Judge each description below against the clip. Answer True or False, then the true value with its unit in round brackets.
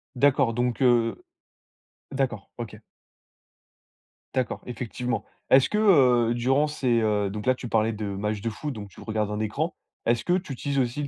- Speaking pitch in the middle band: False (120 Hz)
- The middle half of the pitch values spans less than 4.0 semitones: True (3.6 semitones)